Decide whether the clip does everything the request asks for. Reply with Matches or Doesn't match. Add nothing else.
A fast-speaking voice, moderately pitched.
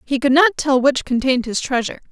Doesn't match